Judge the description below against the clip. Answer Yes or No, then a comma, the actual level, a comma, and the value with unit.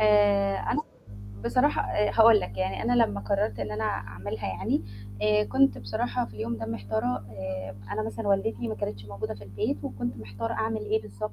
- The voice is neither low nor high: No, low, 110 Hz